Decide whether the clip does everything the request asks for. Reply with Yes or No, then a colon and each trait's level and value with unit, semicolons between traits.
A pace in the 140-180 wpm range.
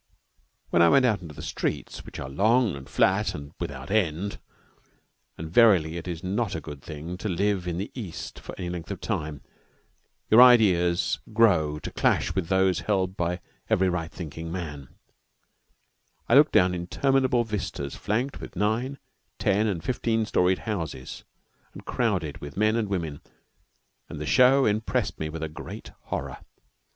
Yes: average, 165 wpm